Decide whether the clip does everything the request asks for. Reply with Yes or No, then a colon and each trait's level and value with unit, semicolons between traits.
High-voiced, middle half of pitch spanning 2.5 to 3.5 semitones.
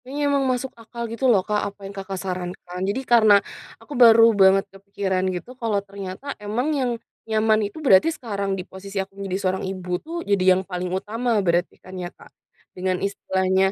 Yes: high, 200 Hz; average, 3.2 semitones